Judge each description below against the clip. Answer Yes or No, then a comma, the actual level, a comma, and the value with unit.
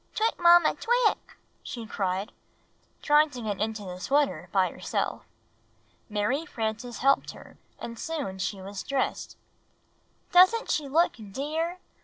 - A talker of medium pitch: No, very high, 255 Hz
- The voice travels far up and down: Yes, wide, 7.8 semitones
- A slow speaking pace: Yes, slow, 130 wpm